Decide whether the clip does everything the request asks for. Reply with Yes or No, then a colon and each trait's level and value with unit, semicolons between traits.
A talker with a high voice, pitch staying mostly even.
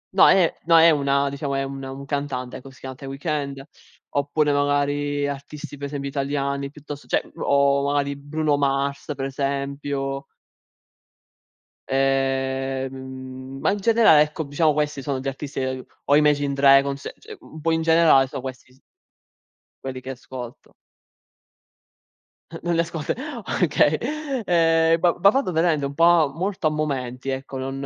No: medium, 140 Hz; narrow, 2.0 semitones